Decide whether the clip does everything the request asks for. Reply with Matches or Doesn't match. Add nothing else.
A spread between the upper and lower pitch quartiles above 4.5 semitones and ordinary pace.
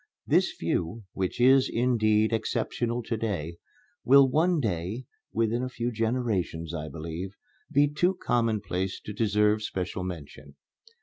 Doesn't match